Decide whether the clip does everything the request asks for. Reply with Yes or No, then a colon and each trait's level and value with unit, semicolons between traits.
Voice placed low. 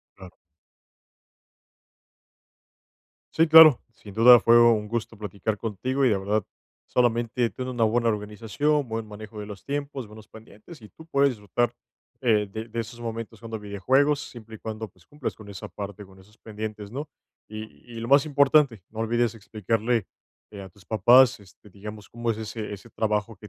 Yes: low, 110 Hz